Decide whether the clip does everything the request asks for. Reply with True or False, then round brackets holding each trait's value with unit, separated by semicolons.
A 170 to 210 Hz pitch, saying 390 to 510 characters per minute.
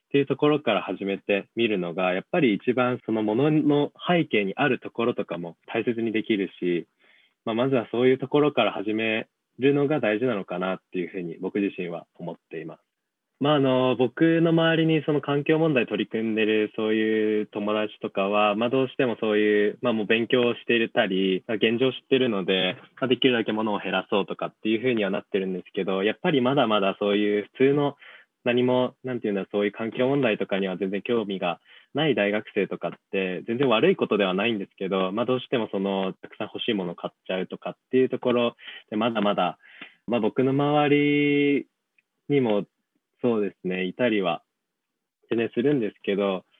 False (115 Hz; 405 characters per minute)